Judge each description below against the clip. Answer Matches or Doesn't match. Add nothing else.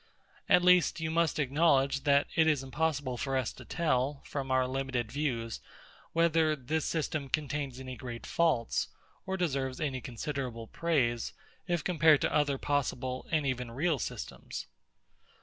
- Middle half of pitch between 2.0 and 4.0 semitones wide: Matches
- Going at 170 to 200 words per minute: Doesn't match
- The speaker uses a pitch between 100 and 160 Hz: Matches